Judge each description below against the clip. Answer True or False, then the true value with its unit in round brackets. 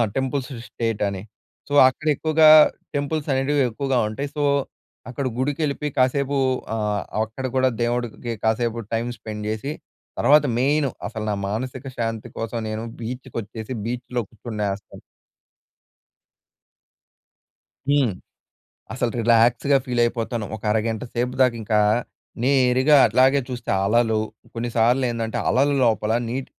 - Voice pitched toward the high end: False (120 Hz)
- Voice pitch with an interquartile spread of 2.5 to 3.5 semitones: True (3.0 semitones)